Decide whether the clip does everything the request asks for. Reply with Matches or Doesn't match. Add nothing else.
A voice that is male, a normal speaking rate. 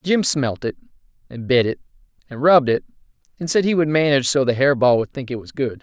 Doesn't match